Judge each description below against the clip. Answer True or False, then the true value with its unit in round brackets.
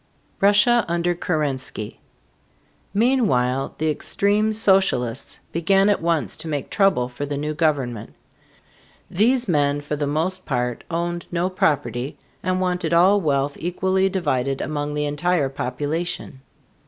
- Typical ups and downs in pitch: True (4.8 semitones)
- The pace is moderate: False (130 wpm)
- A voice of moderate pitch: True (160 Hz)